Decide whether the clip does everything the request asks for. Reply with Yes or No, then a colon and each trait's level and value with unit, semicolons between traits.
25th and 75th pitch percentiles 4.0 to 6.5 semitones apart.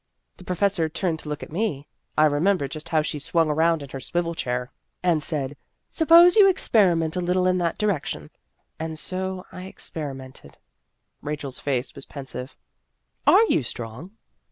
Yes: average, 4.4 semitones